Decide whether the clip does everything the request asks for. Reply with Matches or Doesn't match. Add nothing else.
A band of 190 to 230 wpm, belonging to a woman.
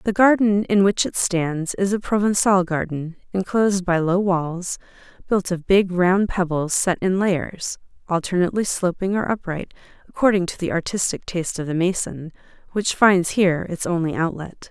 Doesn't match